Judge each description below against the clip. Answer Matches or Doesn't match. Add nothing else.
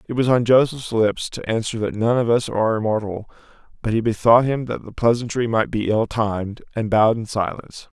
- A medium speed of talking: Doesn't match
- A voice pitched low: Matches